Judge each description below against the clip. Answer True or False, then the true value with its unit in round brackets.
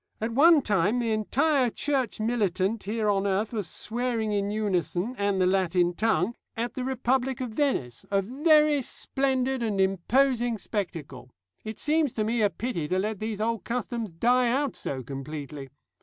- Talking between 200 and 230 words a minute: False (165 wpm)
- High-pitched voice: True (220 Hz)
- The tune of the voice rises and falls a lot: False (4.6 semitones)